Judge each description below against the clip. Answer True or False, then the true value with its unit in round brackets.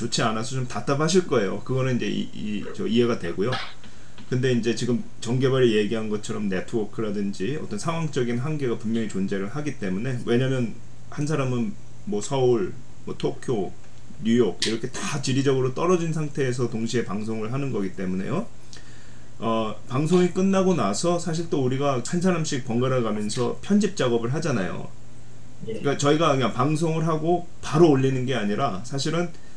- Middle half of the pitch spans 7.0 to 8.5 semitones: False (5.5 semitones)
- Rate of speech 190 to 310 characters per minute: False (355 characters per minute)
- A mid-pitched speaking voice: False (130 Hz)